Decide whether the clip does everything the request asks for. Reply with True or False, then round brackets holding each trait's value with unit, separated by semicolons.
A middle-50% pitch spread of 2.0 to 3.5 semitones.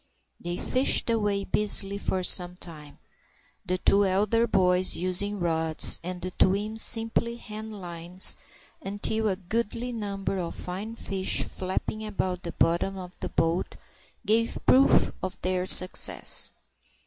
True (2.9 semitones)